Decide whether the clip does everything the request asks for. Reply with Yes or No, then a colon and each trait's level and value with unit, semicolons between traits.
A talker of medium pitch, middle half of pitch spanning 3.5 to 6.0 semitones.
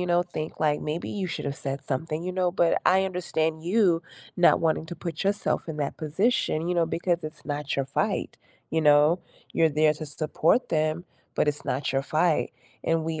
No: medium, 160 Hz; narrow, 2.5 semitones